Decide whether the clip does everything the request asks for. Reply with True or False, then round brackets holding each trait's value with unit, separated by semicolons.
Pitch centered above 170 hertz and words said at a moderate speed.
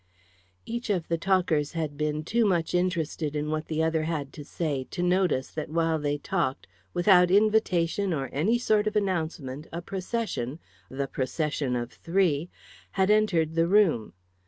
False (165 Hz; 160 wpm)